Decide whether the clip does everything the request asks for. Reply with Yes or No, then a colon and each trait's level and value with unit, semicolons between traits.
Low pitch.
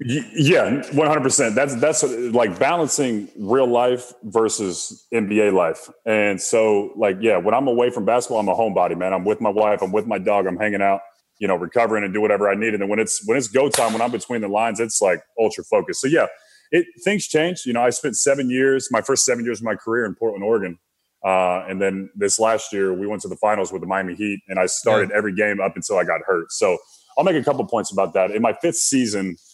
Yes: low, 110 Hz